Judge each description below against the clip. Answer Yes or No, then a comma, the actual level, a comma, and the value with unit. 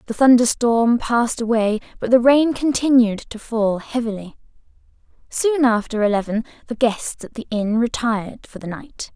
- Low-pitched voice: No, high, 235 Hz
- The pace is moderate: Yes, average, 150 wpm